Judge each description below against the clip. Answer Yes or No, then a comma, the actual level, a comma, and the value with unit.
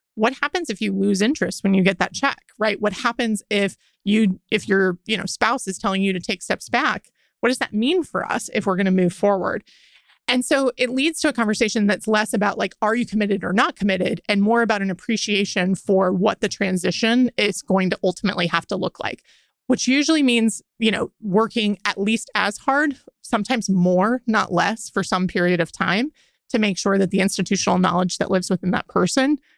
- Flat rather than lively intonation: No, average, 3.4 semitones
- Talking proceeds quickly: Yes, fast, 215 wpm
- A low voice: No, high, 210 Hz